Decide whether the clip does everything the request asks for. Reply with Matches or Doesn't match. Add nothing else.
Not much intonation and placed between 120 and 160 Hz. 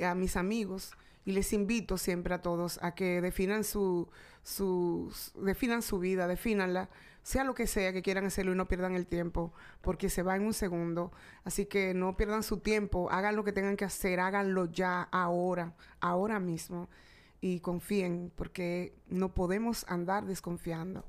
Doesn't match